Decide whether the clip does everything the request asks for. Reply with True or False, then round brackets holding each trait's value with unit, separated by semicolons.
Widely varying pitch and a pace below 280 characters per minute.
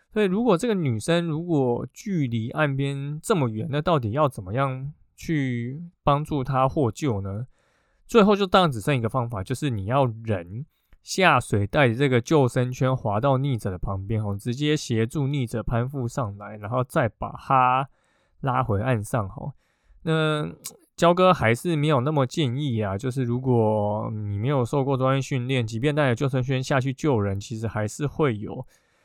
False (4.6 semitones; 260 characters per minute)